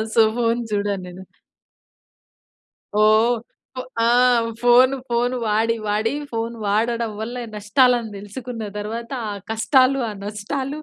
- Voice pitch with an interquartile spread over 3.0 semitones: No, narrow, 2.6 semitones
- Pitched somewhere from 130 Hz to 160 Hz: No, high, 230 Hz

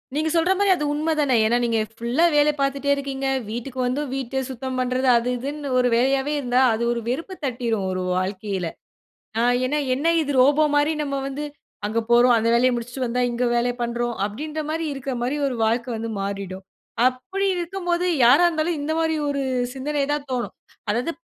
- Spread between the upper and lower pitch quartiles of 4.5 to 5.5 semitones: No, average, 3.8 semitones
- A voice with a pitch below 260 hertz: No, very high, 265 Hz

